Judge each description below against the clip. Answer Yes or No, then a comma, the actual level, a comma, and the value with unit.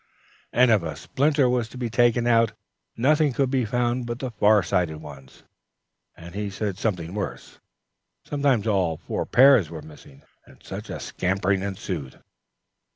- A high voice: No, low, 110 Hz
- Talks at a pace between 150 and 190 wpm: Yes, average, 155 wpm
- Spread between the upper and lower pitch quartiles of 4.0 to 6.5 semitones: Yes, wide, 5.6 semitones